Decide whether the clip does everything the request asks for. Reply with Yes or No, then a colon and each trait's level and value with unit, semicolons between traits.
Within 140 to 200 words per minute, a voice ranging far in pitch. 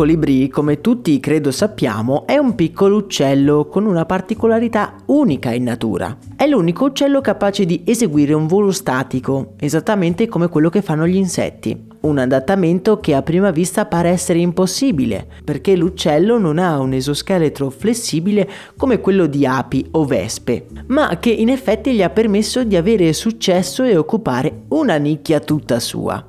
Yes: average, 160 wpm; wide, 6.2 semitones